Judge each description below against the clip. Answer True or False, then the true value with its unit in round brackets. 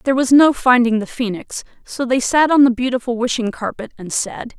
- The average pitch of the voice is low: False (245 Hz)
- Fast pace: True (210 wpm)